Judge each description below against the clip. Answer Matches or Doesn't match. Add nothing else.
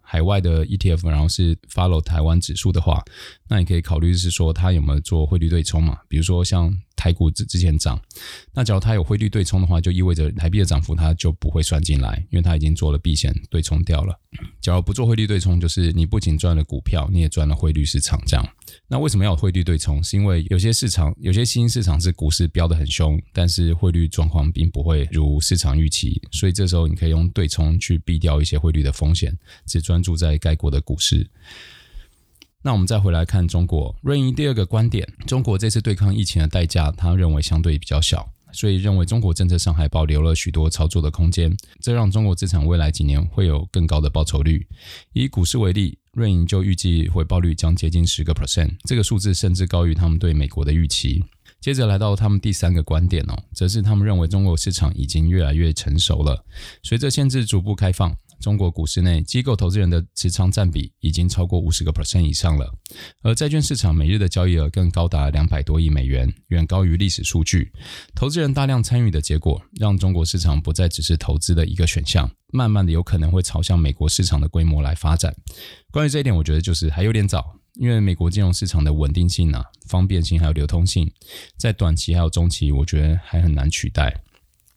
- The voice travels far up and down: Doesn't match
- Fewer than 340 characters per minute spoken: Doesn't match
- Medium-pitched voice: Doesn't match